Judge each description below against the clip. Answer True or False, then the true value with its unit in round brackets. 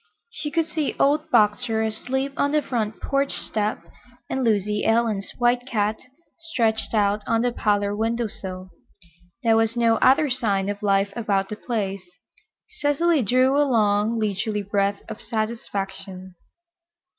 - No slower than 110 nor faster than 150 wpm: True (145 wpm)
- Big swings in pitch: False (3.6 semitones)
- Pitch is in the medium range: False (220 Hz)